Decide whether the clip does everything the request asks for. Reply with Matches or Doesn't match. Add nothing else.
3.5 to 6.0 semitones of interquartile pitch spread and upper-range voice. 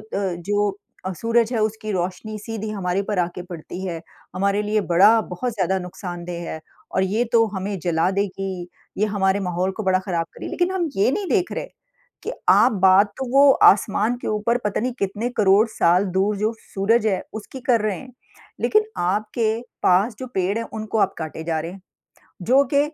Doesn't match